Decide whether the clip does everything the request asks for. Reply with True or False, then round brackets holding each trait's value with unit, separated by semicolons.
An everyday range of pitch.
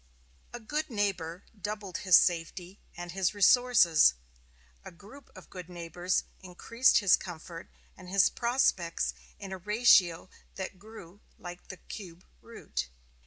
True (3.2 semitones)